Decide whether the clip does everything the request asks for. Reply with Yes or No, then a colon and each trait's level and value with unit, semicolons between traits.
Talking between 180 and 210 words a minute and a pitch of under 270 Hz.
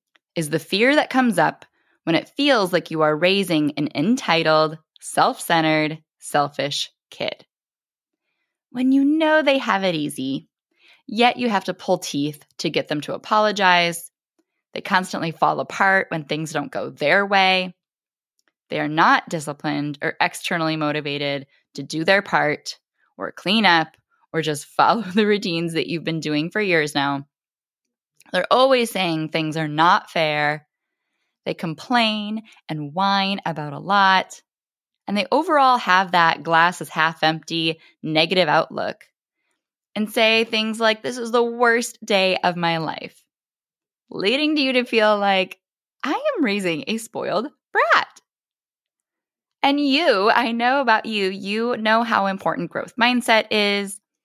No: average, 150 wpm; high, 190 Hz